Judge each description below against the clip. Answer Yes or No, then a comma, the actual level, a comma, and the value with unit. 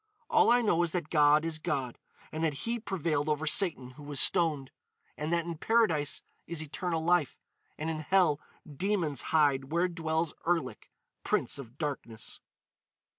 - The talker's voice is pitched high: No, medium, 160 Hz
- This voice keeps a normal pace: Yes, average, 160 wpm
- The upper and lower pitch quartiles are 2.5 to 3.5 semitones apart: Yes, average, 2.9 semitones